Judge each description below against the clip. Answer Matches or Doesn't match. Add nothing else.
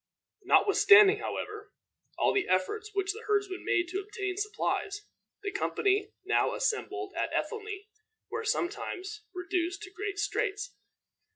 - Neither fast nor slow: Doesn't match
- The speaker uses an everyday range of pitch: Doesn't match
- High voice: Matches